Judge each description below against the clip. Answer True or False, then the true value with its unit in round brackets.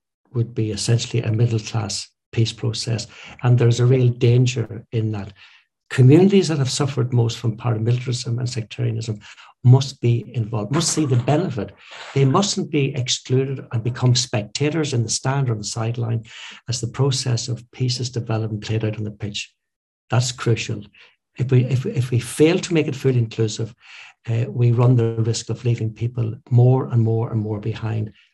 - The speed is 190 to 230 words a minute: False (180 wpm)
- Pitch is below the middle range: True (120 Hz)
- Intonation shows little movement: True (2.3 semitones)